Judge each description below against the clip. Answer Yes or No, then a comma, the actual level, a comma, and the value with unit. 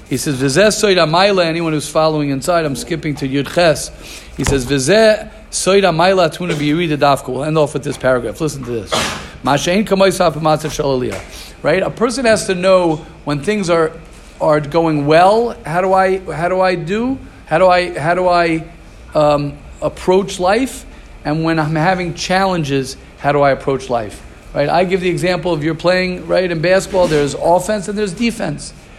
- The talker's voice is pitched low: No, medium, 170 Hz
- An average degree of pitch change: Yes, average, 4.1 semitones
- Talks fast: No, average, 155 wpm